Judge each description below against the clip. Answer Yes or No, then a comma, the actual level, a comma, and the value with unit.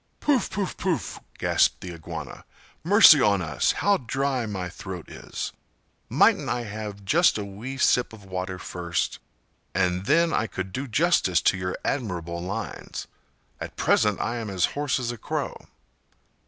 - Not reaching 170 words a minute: Yes, average, 160 wpm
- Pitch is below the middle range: Yes, low, 105 Hz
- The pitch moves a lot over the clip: Yes, wide, 6.6 semitones